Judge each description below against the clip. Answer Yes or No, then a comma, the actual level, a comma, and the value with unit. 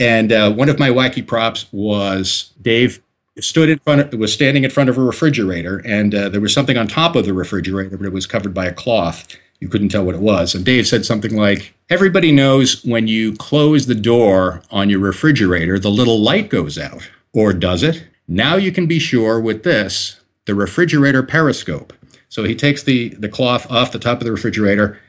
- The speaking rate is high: Yes, fast, 210 wpm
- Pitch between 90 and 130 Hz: Yes, low, 115 Hz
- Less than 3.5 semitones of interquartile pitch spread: No, average, 4.8 semitones